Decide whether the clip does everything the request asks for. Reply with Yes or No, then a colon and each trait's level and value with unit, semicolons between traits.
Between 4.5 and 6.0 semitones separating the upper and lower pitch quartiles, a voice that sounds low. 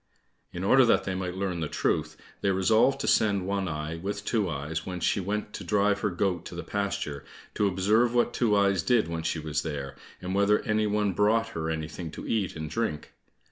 No: average, 4.1 semitones; very low, 95 Hz